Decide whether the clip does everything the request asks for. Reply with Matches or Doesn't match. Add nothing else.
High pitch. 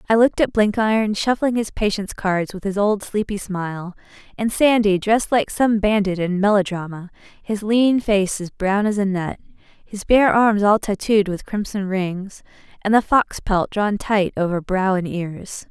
Matches